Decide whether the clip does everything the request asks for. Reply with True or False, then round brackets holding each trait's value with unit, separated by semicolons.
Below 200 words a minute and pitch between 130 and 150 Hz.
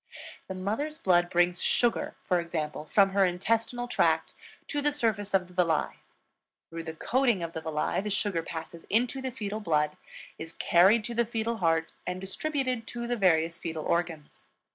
False (175 wpm; 190 Hz)